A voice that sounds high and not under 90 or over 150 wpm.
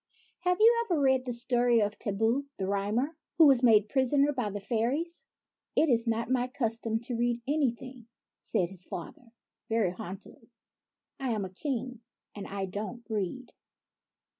No: high, 235 Hz; average, 175 wpm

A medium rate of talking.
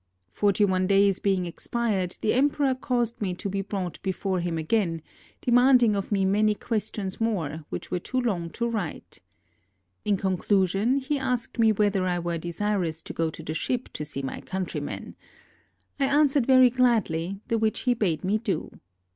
Yes: average, 180 wpm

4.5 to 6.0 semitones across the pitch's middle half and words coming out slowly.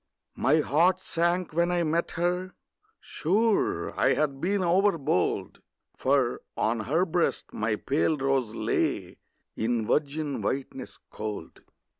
Yes: average, 4.8 semitones; slow, 120 wpm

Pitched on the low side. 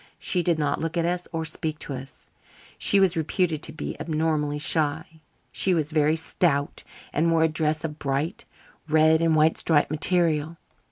No: medium, 160 Hz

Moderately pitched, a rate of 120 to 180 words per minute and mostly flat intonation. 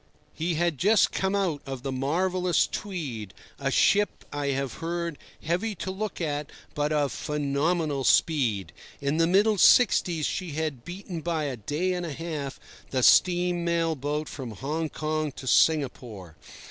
No: medium, 155 Hz; average, 160 wpm; average, 3.9 semitones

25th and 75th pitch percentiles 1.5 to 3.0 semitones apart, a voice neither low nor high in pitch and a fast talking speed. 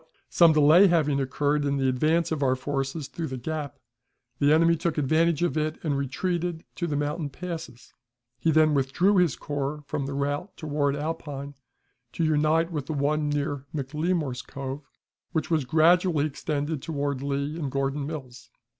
No: narrow, 2.5 semitones; medium, 150 Hz; average, 170 wpm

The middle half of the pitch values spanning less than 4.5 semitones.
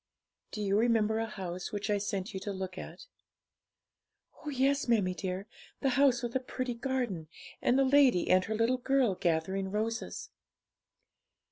No: average, 5.0 semitones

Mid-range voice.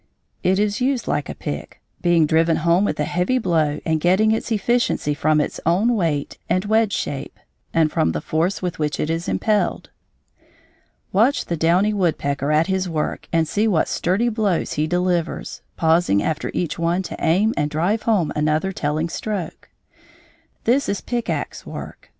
Yes: medium, 175 Hz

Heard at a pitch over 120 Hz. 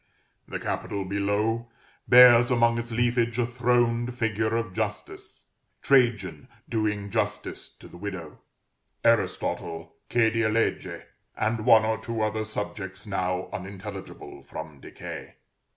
No: low, 110 Hz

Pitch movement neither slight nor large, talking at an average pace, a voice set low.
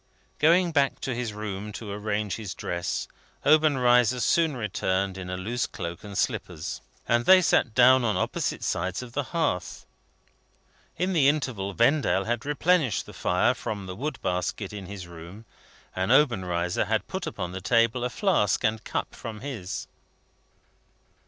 No: wide, 5.8 semitones; average, 160 wpm; low, 110 Hz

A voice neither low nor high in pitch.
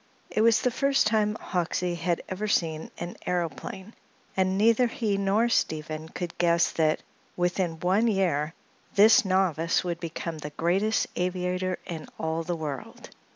Yes: medium, 180 Hz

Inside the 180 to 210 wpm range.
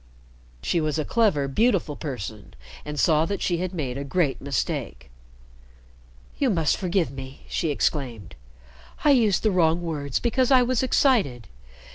No: average, 150 wpm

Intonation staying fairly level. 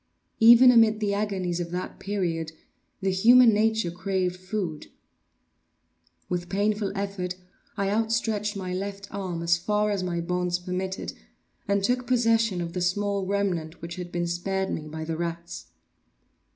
No: average, 3.0 semitones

